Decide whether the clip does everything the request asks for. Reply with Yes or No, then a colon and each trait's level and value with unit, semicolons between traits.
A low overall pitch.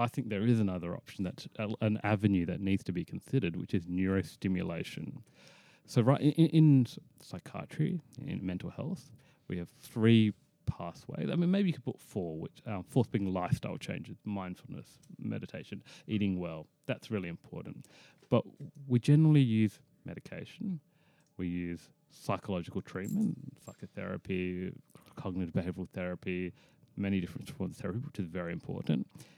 Yes: low, 110 Hz